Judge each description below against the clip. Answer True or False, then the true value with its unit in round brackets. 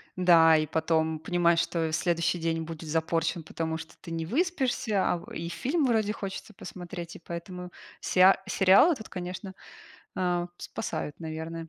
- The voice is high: False (170 Hz)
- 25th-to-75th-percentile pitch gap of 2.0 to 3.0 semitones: True (2.5 semitones)